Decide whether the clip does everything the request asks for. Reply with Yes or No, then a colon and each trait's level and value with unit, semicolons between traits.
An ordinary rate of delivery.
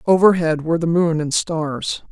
Yes: average, 170 wpm